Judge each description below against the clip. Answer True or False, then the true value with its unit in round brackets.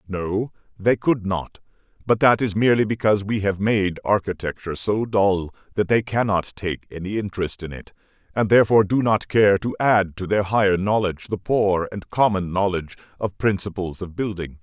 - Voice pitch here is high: False (100 Hz)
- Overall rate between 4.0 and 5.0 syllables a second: False (5.3 syllables/s)